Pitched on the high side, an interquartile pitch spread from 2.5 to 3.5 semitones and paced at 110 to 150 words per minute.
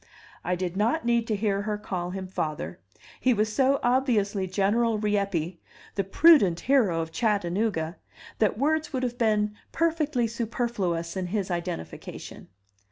No: high, 210 Hz; average, 4.6 semitones; average, 145 wpm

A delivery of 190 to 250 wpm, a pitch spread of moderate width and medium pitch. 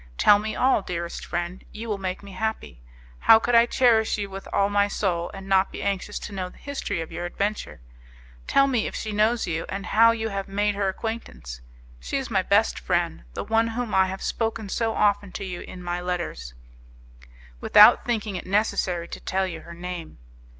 No: fast, 205 wpm; average, 3.6 semitones; high, 200 Hz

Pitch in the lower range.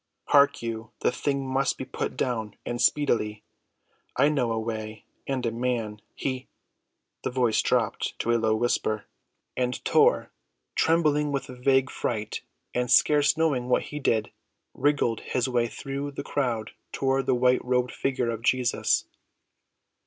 Yes: low, 125 Hz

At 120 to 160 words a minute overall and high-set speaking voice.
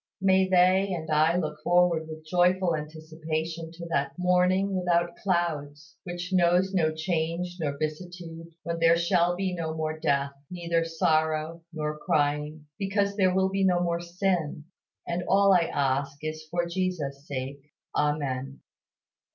No: average, 145 wpm; medium, 170 Hz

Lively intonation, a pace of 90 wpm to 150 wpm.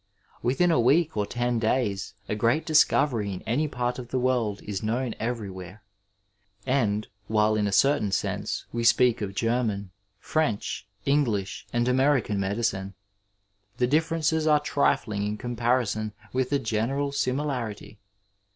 No: average, 4.3 semitones; average, 140 wpm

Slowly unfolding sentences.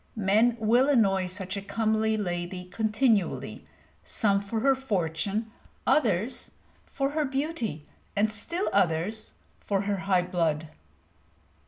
Yes: slow, 120 wpm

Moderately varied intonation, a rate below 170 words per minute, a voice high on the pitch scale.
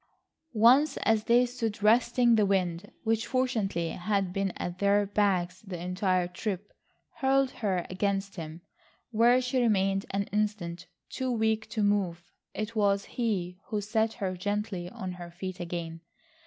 Yes: average, 3.5 semitones; average, 150 wpm; high, 200 Hz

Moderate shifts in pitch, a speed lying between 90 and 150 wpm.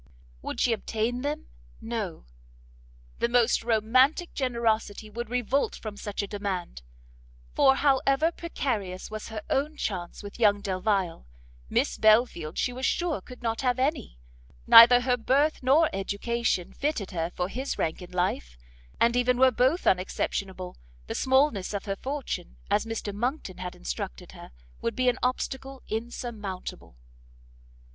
Yes: average, 4.6 semitones; average, 145 wpm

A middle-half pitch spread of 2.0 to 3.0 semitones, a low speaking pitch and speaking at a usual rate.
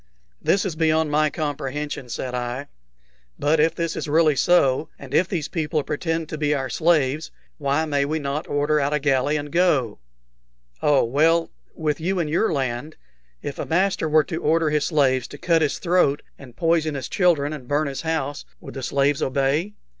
No: narrow, 2.6 semitones; medium, 150 Hz; average, 190 wpm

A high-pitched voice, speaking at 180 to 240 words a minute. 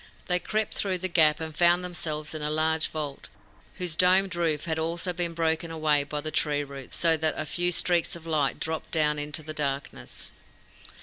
No: medium, 160 Hz; average, 190 wpm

